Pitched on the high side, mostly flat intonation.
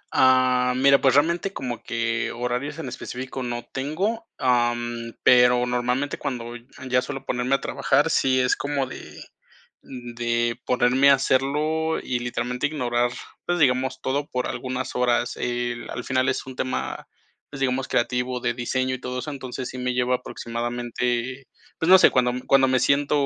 No: low, 125 Hz; narrow, 1.8 semitones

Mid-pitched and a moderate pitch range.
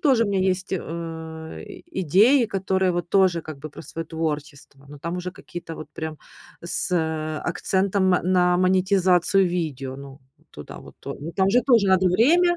Yes: medium, 180 Hz; average, 3.0 semitones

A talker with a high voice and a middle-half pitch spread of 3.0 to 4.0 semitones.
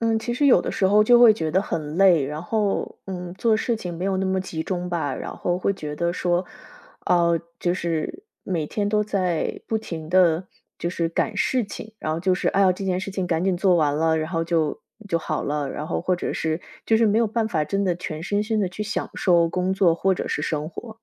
No: medium, 180 Hz; average, 3.6 semitones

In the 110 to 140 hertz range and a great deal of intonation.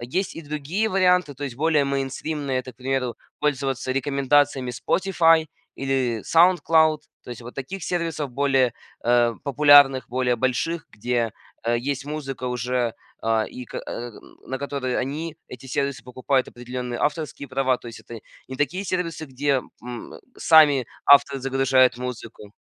No: low, 135 Hz; average, 3.1 semitones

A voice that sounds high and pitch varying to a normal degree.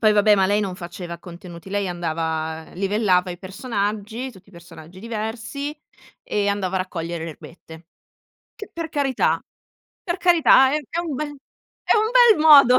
No: high, 200 Hz; wide, 7.2 semitones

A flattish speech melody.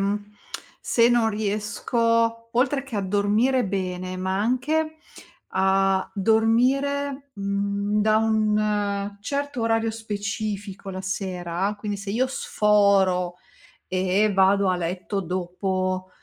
No: average, 3.0 semitones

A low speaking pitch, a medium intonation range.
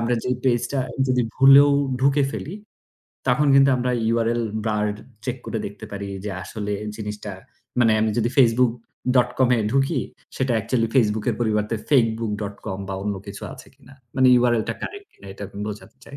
Yes: low, 115 Hz; average, 3.6 semitones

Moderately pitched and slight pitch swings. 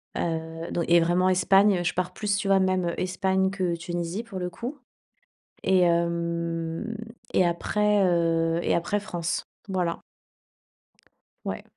Yes: medium, 180 Hz; narrow, 2.3 semitones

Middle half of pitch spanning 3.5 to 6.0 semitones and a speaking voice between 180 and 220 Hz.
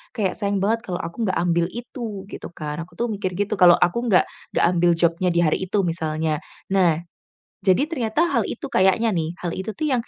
Yes: average, 4.5 semitones; high, 190 Hz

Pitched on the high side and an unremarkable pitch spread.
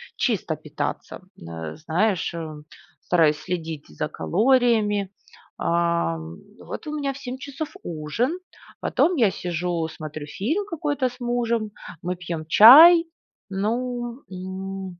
No: high, 195 Hz; wide, 6.9 semitones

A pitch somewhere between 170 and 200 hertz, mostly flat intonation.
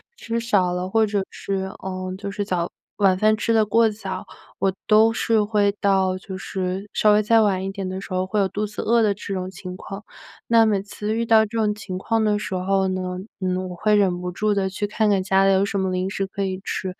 Yes: high, 195 Hz; narrow, 2.2 semitones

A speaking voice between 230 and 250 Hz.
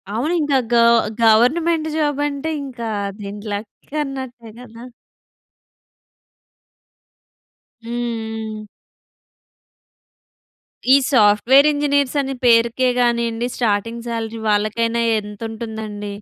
Yes: high, 235 Hz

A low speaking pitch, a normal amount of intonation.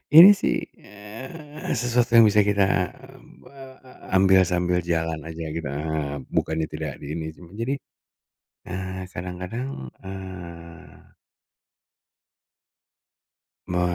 No: very low, 95 Hz; wide, 5.7 semitones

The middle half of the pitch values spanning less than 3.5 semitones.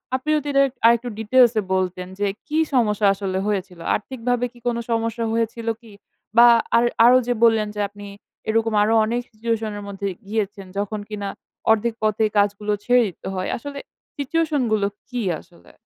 Yes: average, 2.9 semitones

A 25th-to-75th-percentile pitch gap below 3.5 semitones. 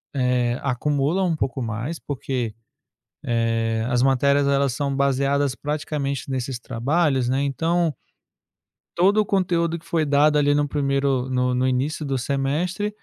Yes: average, 2.9 semitones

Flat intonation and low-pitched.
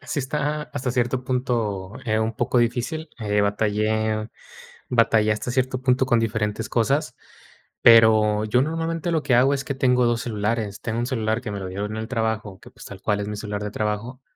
No: average, 3.1 semitones; low, 115 Hz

